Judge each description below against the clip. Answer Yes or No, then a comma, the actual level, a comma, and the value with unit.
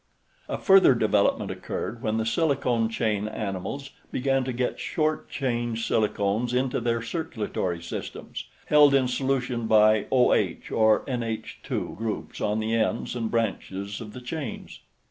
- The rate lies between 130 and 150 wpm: Yes, average, 140 wpm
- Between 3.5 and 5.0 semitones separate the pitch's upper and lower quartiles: No, average, 3.1 semitones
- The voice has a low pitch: Yes, low, 115 Hz